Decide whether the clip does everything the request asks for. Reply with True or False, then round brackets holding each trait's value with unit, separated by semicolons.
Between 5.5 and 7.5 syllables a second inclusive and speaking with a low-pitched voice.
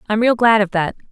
False (6.2 syllables/s; 215 Hz)